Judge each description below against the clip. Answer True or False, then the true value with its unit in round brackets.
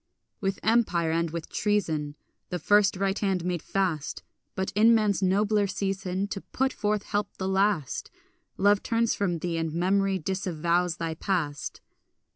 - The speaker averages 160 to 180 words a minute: False (150 wpm)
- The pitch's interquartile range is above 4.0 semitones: False (3.2 semitones)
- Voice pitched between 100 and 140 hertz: False (190 Hz)